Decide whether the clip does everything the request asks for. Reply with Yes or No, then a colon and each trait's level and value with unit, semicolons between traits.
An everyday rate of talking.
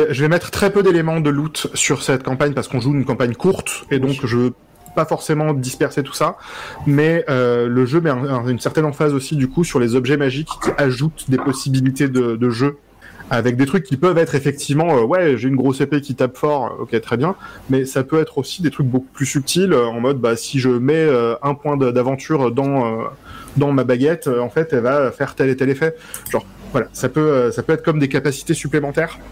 No: fast, 235 wpm